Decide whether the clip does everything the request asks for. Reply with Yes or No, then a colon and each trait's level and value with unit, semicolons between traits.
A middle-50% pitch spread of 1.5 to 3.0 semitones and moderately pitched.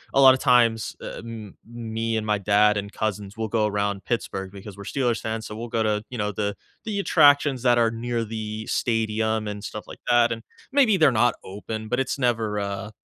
No: narrow, 2.4 semitones; low, 110 Hz